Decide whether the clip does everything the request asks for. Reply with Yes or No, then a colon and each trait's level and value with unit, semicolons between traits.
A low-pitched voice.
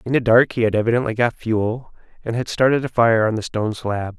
Yes: low, 115 Hz